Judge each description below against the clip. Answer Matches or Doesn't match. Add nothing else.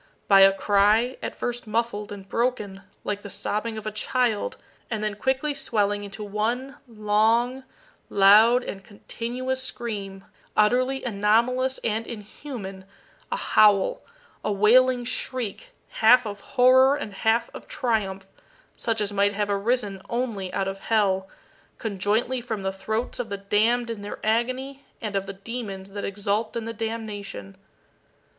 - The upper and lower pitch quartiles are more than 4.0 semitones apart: Doesn't match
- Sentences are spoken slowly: Doesn't match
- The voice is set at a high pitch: Matches